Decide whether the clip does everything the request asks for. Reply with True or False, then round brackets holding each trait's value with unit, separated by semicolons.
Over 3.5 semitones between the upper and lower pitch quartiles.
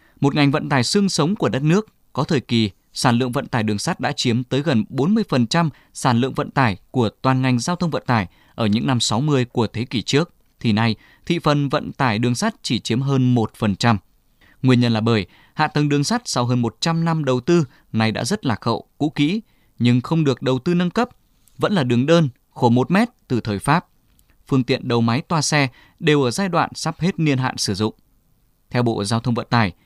True (4.7 semitones)